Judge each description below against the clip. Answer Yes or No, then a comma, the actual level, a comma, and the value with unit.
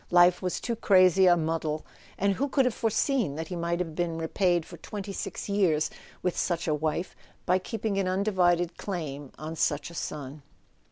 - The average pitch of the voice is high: No, medium, 175 Hz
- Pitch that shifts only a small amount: No, average, 3.4 semitones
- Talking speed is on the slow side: No, average, 180 wpm